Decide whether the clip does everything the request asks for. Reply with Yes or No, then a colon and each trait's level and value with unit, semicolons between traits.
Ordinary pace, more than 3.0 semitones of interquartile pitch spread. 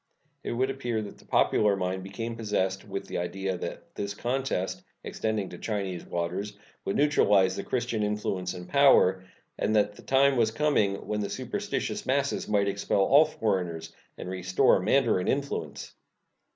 Yes: average, 160 wpm; average, 4.6 semitones